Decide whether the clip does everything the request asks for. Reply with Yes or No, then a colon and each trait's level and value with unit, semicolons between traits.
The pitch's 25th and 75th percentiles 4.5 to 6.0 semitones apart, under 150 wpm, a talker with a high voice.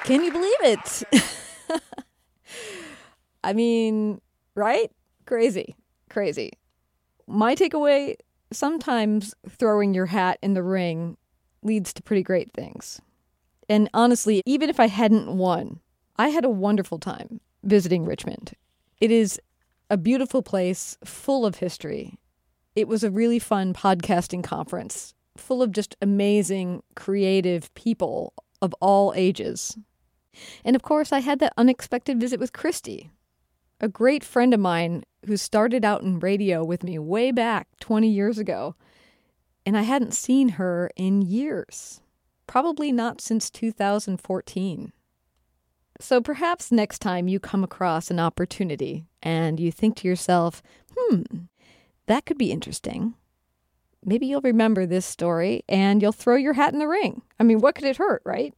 Yes: average, 5.1 semitones; average, 140 wpm; high, 210 Hz